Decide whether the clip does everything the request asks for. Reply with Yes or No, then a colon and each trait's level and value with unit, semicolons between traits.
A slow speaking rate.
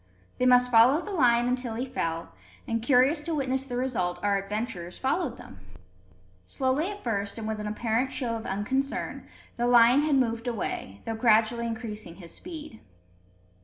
No: average, 165 wpm